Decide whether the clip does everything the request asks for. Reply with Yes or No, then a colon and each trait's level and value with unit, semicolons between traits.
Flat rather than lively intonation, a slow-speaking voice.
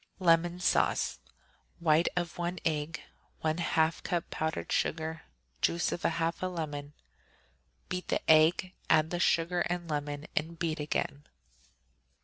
Yes: narrow, 1.8 semitones; slow, 125 wpm